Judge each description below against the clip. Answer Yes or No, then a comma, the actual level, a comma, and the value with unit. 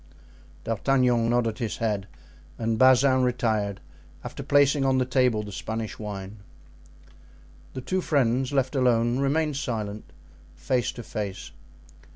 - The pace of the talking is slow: Yes, slow, 125 wpm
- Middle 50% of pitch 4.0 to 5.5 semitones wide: No, average, 3.3 semitones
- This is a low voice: Yes, low, 120 Hz